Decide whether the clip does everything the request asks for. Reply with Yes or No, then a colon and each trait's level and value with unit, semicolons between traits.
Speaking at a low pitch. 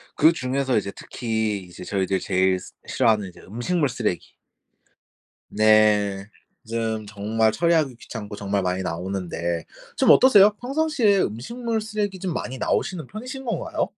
Yes: low, 115 Hz